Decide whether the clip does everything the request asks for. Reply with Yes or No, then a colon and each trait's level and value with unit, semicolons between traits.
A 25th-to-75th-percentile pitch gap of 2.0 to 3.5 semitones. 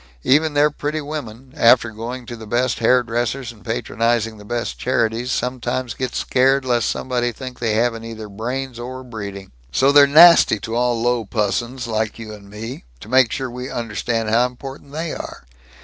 Yes: narrow, 2.4 semitones